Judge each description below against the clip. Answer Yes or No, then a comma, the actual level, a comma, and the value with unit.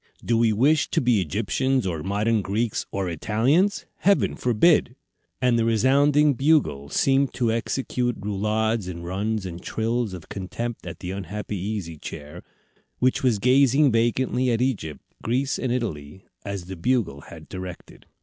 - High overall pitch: No, low, 115 Hz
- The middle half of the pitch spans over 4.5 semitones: Yes, average, 4.9 semitones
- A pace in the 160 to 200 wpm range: No, average, 150 wpm